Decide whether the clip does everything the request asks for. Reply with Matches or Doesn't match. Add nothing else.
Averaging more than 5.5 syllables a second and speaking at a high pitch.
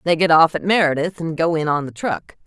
Doesn't match